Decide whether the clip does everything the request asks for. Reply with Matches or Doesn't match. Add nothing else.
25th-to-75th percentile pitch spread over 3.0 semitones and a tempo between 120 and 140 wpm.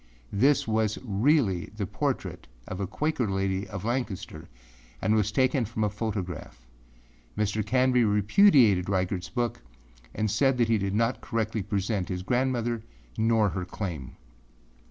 Matches